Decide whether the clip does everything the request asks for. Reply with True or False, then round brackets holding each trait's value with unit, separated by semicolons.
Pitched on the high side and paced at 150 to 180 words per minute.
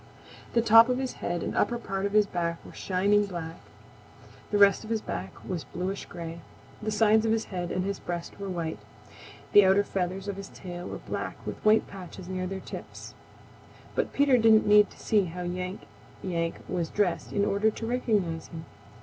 False (195 Hz; 195 wpm)